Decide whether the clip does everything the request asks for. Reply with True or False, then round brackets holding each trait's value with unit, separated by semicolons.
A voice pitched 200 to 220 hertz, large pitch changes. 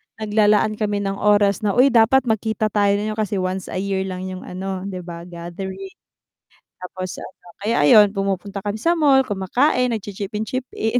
False (205 Hz; 2.5 semitones)